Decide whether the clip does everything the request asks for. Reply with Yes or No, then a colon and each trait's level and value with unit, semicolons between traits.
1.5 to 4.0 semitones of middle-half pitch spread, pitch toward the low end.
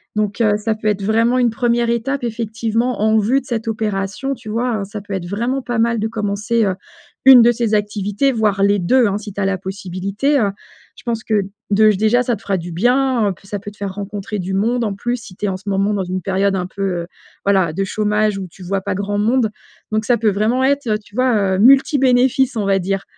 No: average, 3.1 semitones; high, 210 Hz